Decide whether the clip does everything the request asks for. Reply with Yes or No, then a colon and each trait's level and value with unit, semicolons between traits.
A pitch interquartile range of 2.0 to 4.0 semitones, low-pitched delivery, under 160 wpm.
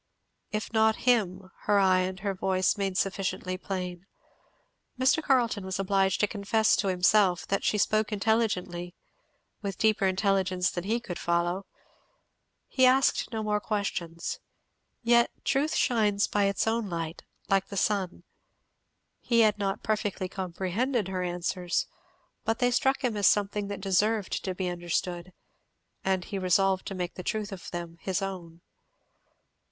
No: average, 2.8 semitones; high, 195 Hz; average, 150 wpm